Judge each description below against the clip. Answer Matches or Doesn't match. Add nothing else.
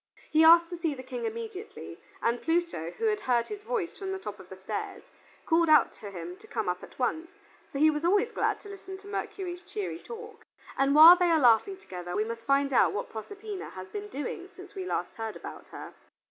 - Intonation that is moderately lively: Doesn't match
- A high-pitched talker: Matches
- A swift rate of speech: Matches